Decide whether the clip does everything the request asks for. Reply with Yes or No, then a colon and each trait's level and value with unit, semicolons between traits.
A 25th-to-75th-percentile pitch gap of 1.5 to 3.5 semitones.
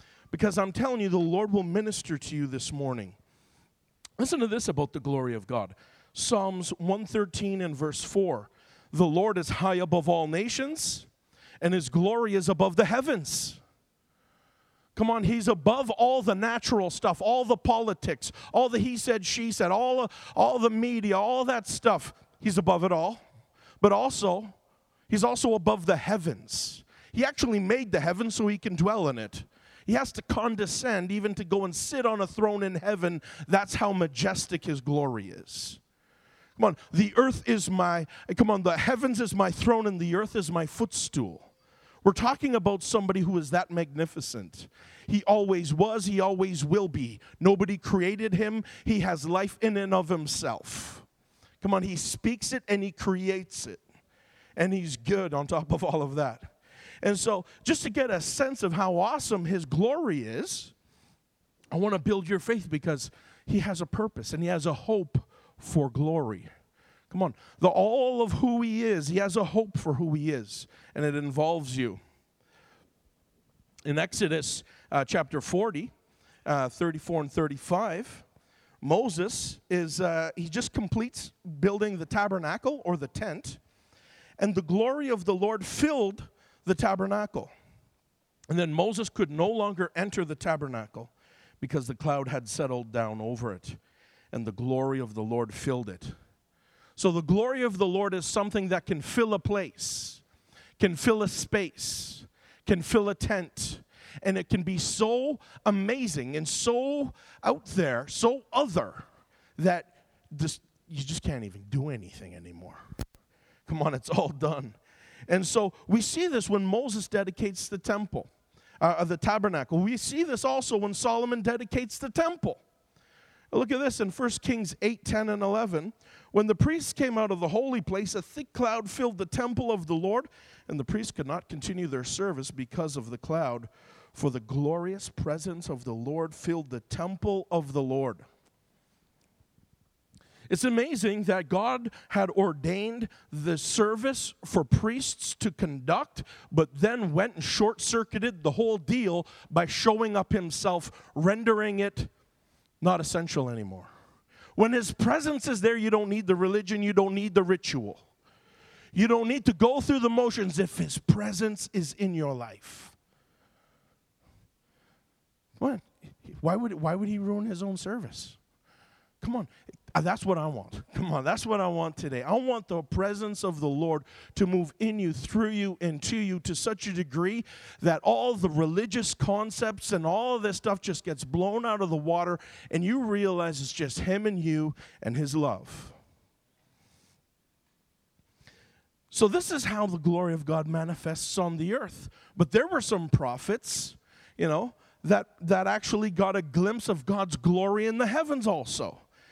No: average, 5.2 semitones